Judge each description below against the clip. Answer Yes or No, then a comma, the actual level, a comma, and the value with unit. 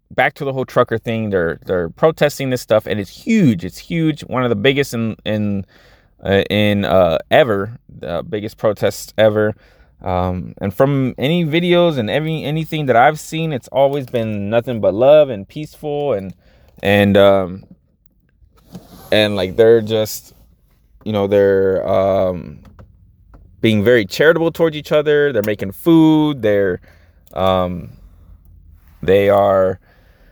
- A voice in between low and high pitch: No, low, 105 Hz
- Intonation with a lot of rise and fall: Yes, wide, 6.5 semitones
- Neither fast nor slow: Yes, average, 145 wpm